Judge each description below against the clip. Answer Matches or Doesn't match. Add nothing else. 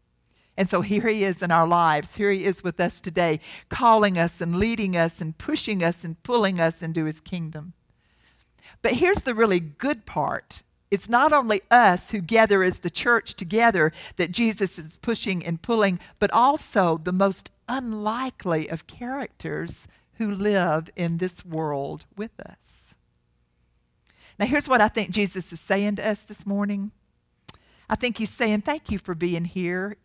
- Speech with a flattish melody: Doesn't match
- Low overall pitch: Doesn't match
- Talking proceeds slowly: Doesn't match